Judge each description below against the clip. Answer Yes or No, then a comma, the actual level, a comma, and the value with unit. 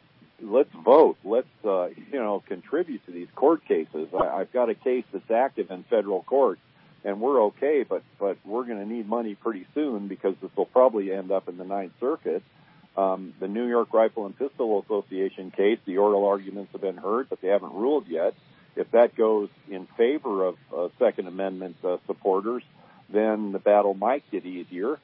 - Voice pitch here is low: Yes, low, 105 Hz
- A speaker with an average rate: Yes, average, 190 wpm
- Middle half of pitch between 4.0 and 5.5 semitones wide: Yes, average, 4.9 semitones